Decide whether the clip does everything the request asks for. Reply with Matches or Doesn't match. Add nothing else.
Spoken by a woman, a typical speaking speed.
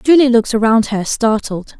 Matches